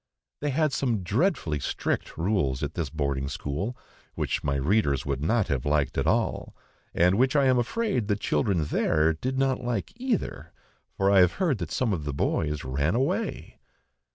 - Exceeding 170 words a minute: Yes, average, 180 wpm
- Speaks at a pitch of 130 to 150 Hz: No, very low, 95 Hz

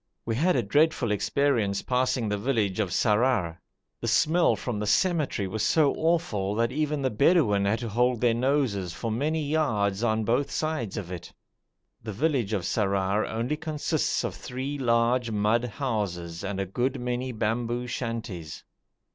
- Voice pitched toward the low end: Yes, low, 115 Hz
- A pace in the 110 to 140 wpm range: No, average, 165 wpm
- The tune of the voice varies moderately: Yes, average, 4.8 semitones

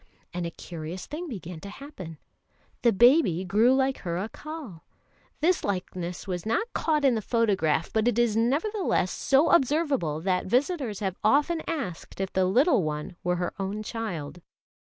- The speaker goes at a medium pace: Yes, average, 155 wpm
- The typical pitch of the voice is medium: No, high, 215 Hz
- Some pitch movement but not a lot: No, wide, 7.5 semitones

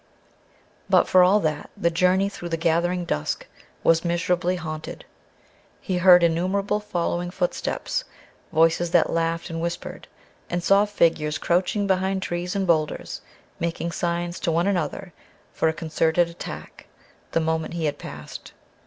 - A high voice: No, medium, 170 Hz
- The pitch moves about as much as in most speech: No, narrow, 1.8 semitones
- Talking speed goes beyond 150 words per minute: No, average, 145 wpm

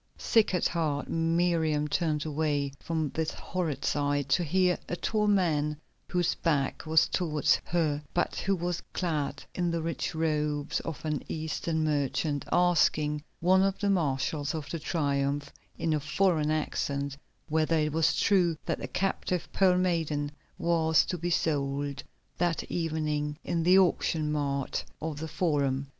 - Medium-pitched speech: Yes, medium, 160 Hz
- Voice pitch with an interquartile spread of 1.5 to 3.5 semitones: Yes, average, 2.8 semitones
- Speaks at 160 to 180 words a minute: No, average, 150 wpm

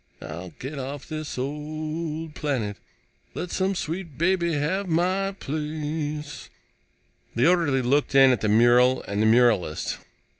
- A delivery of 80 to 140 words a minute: Yes, slow, 135 wpm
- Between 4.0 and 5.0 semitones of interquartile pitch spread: Yes, average, 4.5 semitones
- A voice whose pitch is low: No, medium, 150 Hz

